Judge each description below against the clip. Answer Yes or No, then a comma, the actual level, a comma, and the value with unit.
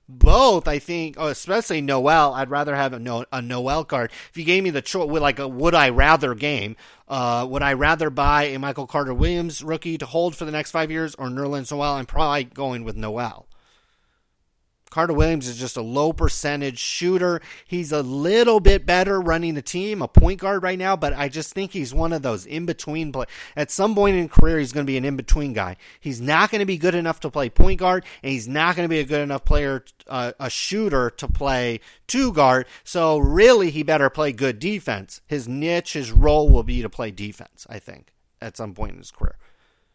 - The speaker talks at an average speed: No, fast, 220 wpm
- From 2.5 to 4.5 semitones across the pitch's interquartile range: Yes, average, 4.1 semitones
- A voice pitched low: No, medium, 145 Hz